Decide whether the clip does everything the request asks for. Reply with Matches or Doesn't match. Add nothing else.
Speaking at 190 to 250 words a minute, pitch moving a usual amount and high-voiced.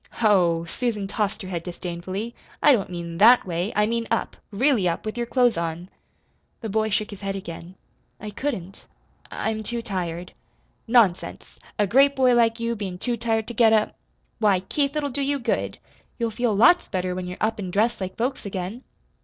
Matches